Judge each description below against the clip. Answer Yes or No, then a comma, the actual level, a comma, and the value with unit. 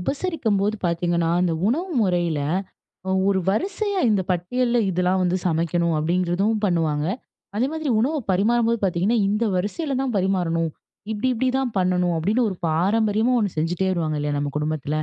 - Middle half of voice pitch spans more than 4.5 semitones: Yes, average, 4.9 semitones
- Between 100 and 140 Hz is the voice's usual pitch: No, medium, 185 Hz